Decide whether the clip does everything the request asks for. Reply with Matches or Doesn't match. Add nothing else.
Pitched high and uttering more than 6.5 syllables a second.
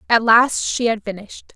Doesn't match